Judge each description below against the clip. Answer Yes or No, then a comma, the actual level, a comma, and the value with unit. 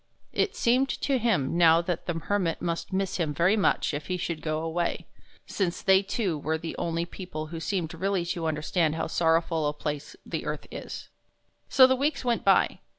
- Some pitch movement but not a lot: Yes, average, 3.4 semitones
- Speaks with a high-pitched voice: No, medium, 170 Hz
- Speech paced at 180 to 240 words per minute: Yes, average, 195 wpm